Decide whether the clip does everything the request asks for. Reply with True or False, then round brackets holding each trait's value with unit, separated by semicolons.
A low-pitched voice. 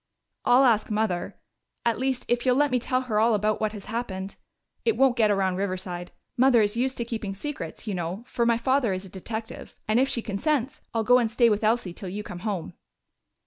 False (220 Hz)